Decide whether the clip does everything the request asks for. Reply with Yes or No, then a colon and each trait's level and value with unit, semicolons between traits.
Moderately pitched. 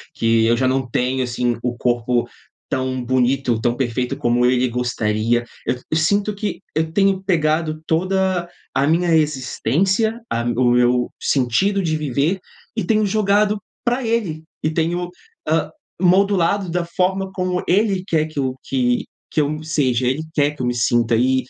Yes: medium, 155 Hz